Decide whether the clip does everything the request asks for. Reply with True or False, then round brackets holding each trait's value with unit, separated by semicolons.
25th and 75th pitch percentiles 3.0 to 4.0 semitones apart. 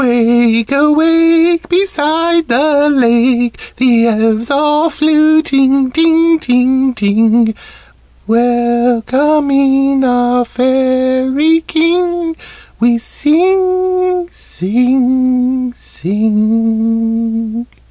False (4.8 semitones)